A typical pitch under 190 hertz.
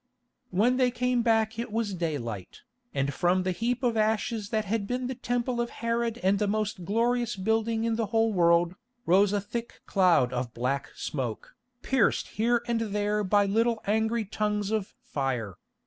No: high, 215 Hz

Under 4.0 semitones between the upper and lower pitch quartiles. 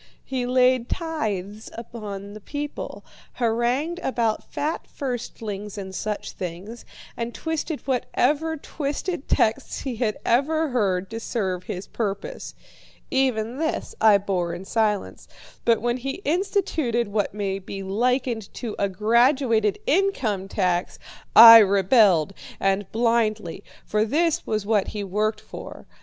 No: average, 4.5 semitones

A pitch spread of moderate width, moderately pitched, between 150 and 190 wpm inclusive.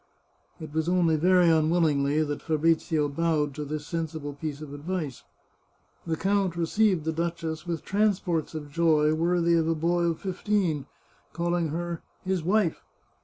No: narrow, 2.1 semitones; medium, 165 Hz; average, 155 wpm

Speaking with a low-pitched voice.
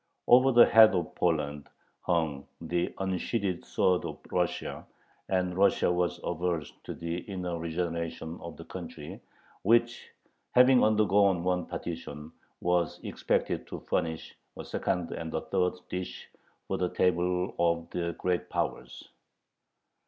Yes: very low, 90 Hz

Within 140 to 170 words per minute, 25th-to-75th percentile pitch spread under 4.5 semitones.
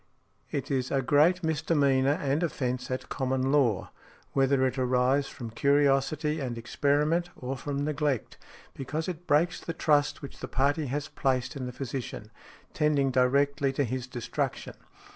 Yes: average, 150 wpm; narrow, 2.4 semitones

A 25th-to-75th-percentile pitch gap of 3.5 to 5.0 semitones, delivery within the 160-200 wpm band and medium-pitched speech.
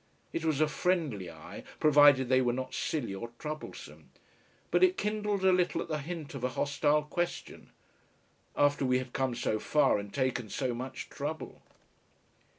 Yes: average, 3.8 semitones; average, 165 wpm; medium, 145 Hz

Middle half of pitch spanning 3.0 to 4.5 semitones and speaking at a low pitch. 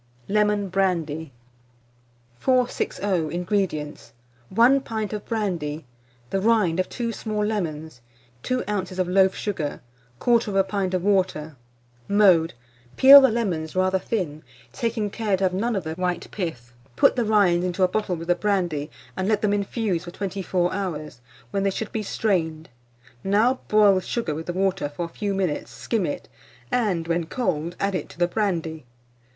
No: average, 3.8 semitones; high, 190 Hz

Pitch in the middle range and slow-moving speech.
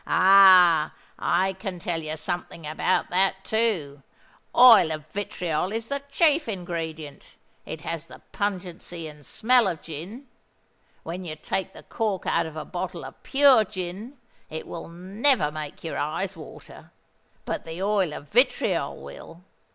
No: medium, 180 Hz; average, 150 wpm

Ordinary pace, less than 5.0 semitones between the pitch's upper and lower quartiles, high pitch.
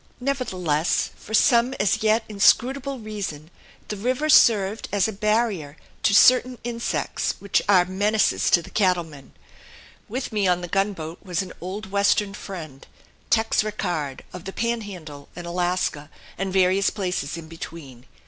Yes: average, 145 wpm; average, 4.2 semitones; high, 195 Hz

